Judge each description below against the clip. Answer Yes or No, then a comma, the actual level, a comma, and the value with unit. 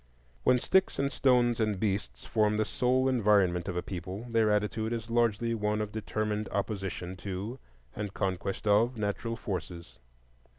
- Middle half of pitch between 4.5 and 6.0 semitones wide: No, average, 2.9 semitones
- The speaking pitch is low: Yes, low, 105 Hz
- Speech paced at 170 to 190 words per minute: No, average, 155 wpm